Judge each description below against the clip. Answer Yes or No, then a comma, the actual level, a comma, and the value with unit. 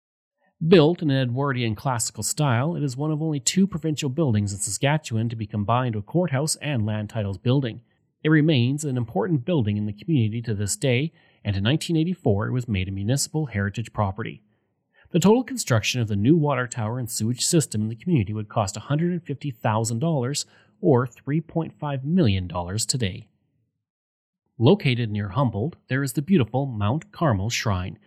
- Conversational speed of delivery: Yes, average, 165 wpm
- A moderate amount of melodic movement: No, wide, 6.2 semitones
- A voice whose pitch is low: Yes, low, 130 Hz